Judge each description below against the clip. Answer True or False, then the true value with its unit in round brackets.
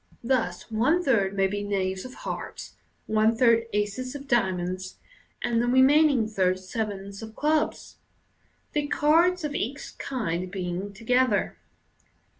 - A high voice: True (220 Hz)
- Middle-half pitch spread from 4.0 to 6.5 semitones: True (5.2 semitones)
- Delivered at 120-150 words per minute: True (140 wpm)